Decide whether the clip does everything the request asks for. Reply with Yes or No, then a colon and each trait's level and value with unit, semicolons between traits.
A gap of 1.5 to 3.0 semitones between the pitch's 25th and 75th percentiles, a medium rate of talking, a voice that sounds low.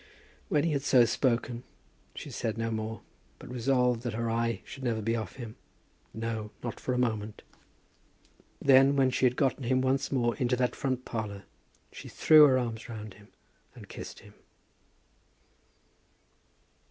Yes: narrow, 2.5 semitones; average, 160 wpm; low, 120 Hz